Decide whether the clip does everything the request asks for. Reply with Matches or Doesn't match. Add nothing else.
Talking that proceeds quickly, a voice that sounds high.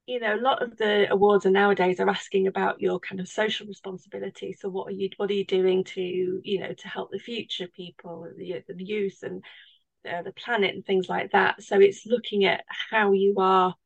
Matches